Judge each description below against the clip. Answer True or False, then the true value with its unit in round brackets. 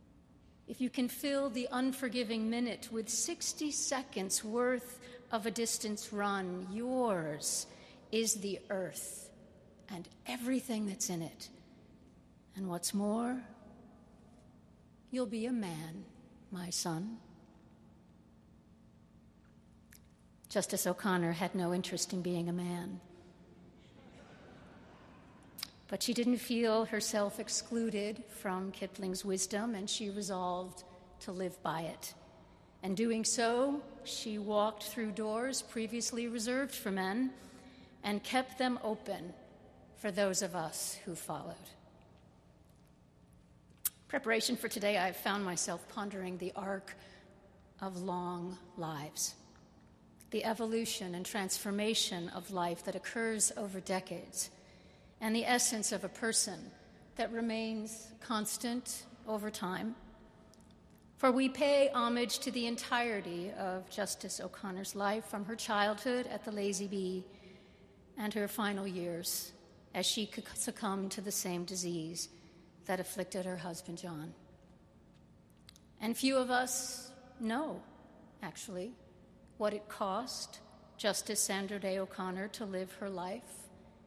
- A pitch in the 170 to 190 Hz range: False (205 Hz)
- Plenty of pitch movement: False (3.7 semitones)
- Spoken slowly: True (115 wpm)